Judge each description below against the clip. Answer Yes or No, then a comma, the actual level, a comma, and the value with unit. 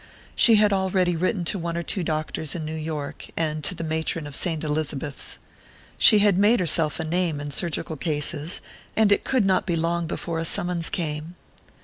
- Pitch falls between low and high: Yes, medium, 165 Hz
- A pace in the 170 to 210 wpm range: Yes, average, 195 wpm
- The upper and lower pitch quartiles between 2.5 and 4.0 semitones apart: Yes, average, 2.9 semitones